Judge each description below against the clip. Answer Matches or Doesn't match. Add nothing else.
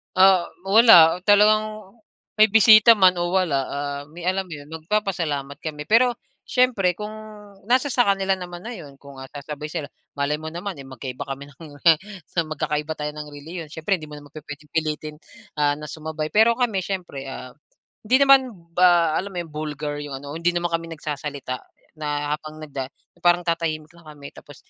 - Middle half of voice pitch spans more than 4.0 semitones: Matches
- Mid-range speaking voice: Matches